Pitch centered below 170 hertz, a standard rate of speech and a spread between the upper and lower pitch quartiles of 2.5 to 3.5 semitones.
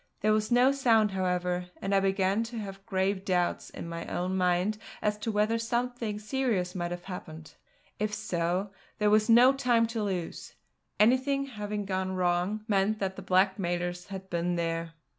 No: high, 195 Hz; average, 170 wpm; average, 3.2 semitones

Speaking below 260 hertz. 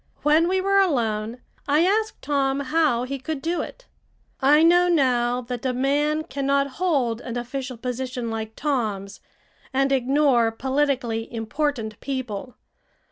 No: very high, 270 Hz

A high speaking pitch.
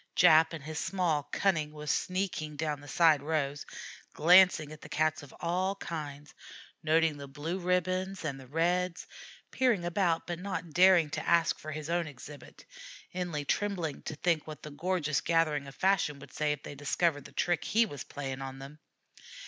No: medium, 155 Hz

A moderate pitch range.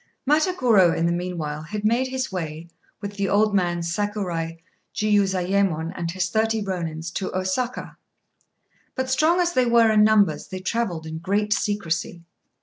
Yes: average, 4.3 semitones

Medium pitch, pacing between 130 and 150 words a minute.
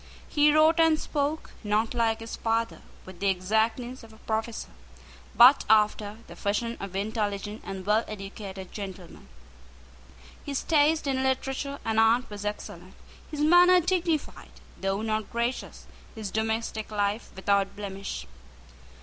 No: high, 220 Hz; slow, 135 wpm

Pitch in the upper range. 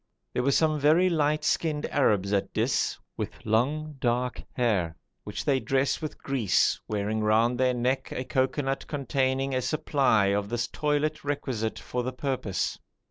No: low, 130 Hz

